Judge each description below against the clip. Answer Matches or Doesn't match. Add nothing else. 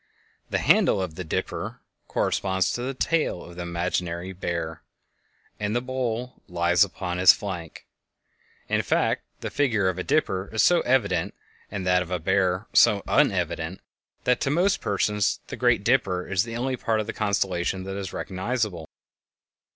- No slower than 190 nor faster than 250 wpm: Doesn't match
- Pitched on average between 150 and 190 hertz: Doesn't match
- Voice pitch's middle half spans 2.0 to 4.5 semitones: Matches